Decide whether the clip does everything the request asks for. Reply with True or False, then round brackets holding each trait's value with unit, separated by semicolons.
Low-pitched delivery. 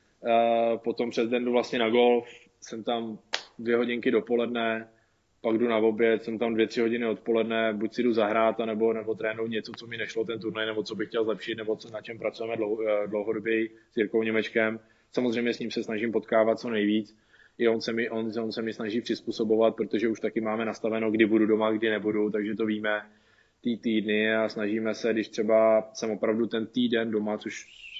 True (110 Hz)